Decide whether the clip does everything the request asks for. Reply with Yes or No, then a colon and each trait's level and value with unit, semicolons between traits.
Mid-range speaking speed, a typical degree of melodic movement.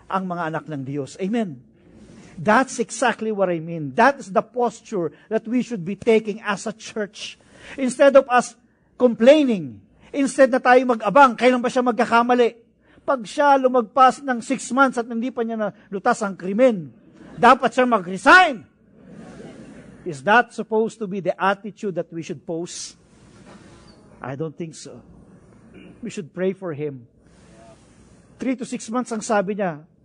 Yes: average, 160 wpm; average, 4.7 semitones